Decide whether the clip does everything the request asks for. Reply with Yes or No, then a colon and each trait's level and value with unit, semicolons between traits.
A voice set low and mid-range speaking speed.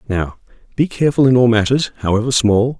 Yes: low, 120 Hz; average, 170 wpm